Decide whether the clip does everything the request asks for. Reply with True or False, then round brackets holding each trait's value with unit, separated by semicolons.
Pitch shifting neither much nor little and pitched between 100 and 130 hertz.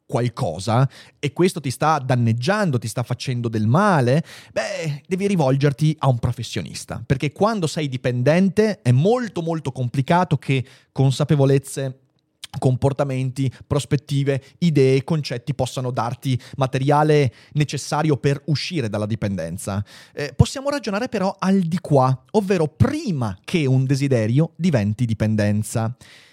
False (3.9 semitones; 140 Hz)